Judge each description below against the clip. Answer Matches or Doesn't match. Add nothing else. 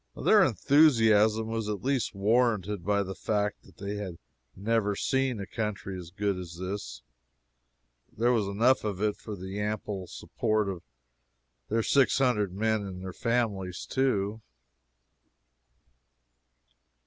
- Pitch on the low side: Matches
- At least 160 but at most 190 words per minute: Doesn't match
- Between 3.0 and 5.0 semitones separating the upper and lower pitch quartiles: Doesn't match